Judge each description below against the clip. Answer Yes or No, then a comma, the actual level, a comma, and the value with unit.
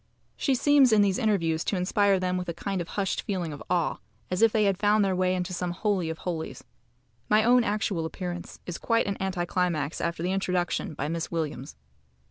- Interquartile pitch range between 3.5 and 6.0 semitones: No, average, 3.1 semitones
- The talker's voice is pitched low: No, medium, 185 Hz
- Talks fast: Yes, fast, 210 wpm